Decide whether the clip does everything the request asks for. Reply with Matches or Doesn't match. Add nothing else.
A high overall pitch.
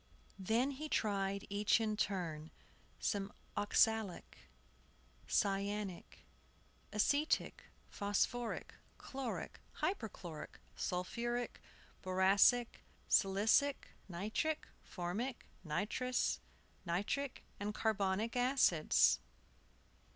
Matches